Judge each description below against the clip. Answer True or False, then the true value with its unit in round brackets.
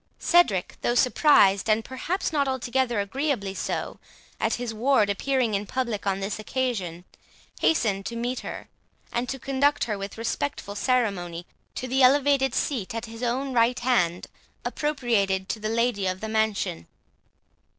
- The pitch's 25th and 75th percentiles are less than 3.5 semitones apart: False (4.6 semitones)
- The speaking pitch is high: True (235 Hz)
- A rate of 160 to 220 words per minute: False (150 wpm)